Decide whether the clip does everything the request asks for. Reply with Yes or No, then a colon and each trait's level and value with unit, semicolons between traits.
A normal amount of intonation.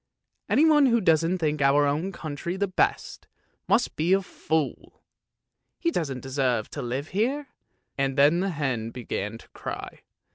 No: wide, 5.8 semitones